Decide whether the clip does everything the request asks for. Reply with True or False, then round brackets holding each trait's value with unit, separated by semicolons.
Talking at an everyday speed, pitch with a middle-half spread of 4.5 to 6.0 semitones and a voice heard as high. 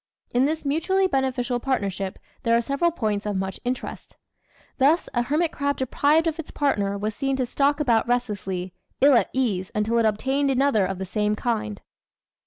True (180 wpm; 5.2 semitones; 245 Hz)